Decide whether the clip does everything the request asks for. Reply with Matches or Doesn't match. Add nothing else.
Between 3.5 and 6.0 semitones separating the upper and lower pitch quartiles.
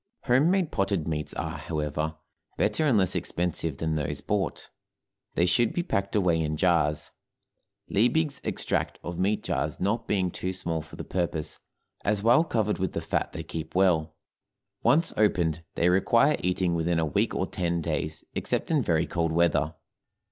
Matches